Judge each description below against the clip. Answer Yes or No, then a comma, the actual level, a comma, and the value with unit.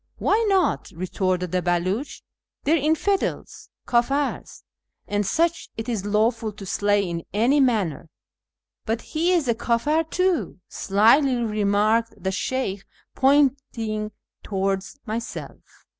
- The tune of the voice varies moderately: No, wide, 5.8 semitones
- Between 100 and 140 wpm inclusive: Yes, slow, 135 wpm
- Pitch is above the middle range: Yes, high, 225 Hz